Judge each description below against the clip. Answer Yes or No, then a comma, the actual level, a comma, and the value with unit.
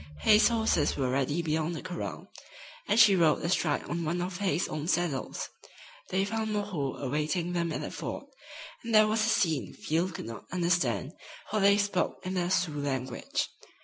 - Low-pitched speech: No, medium, 175 Hz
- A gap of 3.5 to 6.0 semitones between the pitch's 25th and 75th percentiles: Yes, average, 4.9 semitones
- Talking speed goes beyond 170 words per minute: Yes, average, 180 wpm